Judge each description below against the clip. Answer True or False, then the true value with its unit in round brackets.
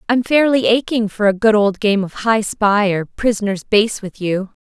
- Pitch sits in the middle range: False (210 Hz)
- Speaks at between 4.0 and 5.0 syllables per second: True (4.6 syllables/s)